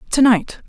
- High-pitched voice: Yes, high, 240 Hz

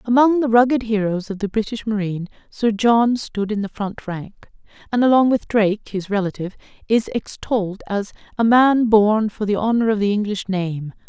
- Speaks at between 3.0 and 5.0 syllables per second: No, 5.2 syllables/s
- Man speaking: No, female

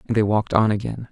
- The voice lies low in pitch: Yes, low, 105 Hz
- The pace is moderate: No, fast, 270 wpm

